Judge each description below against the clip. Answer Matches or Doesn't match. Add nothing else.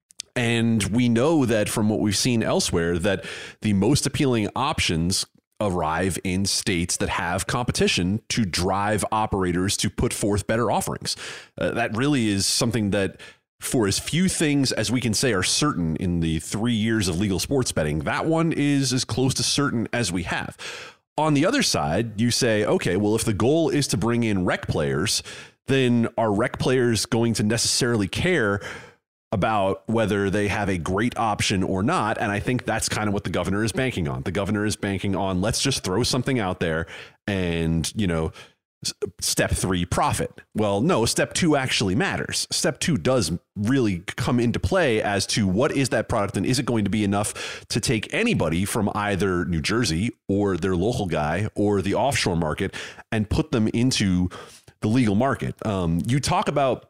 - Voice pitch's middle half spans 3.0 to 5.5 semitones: Matches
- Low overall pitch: Matches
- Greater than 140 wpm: Matches